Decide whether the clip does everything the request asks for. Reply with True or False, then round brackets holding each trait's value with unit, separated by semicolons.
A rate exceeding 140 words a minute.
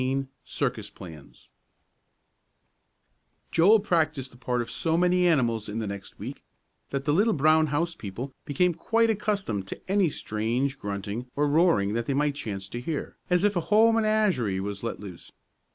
True (165 wpm)